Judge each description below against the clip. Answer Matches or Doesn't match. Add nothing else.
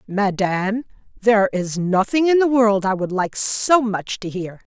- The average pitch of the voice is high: Matches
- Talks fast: Doesn't match